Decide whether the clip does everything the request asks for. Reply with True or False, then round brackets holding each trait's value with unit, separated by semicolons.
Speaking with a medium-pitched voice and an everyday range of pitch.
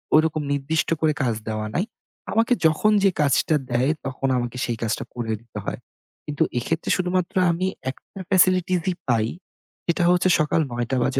False (155 Hz; 6.6 semitones)